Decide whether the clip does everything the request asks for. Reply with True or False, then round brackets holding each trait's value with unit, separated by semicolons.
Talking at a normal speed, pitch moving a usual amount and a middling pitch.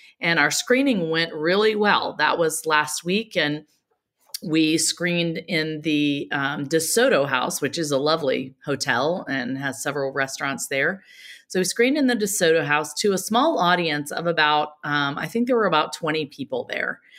True (175 wpm; 3.9 semitones; 160 Hz)